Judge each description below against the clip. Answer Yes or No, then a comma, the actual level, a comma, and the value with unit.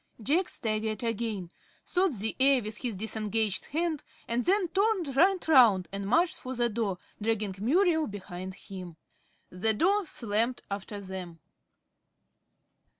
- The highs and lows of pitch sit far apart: Yes, wide, 7.4 semitones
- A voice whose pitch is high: Yes, high, 225 Hz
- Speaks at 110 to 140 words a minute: Yes, slow, 135 wpm